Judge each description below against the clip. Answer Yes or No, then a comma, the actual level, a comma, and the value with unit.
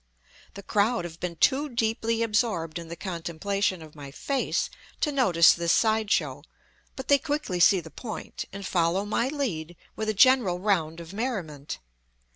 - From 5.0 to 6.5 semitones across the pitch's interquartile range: Yes, wide, 5.5 semitones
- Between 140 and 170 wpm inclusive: Yes, average, 165 wpm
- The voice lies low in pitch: No, high, 200 Hz